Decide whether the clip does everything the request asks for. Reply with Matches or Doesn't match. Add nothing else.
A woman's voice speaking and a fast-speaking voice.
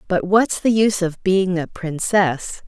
Doesn't match